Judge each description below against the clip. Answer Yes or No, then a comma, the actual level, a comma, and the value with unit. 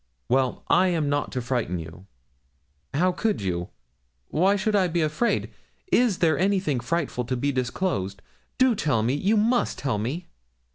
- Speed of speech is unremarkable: Yes, average, 160 wpm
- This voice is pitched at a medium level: Yes, medium, 150 Hz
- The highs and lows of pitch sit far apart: Yes, wide, 7.4 semitones